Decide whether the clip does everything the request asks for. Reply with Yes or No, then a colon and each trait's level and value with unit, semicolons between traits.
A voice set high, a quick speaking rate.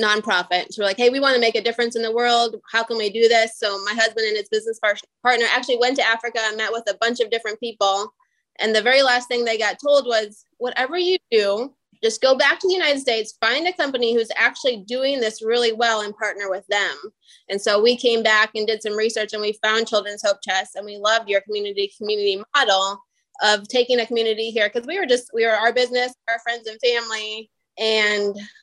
Yes: high, 230 Hz; fast, 235 wpm